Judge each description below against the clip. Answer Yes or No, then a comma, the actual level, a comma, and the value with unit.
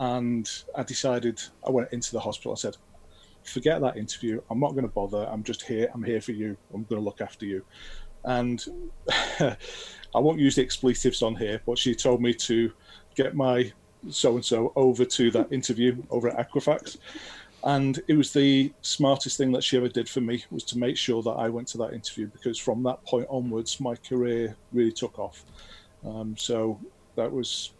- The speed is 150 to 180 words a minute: No, average, 200 wpm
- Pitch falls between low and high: No, low, 120 Hz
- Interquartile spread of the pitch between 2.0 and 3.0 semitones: Yes, narrow, 2.5 semitones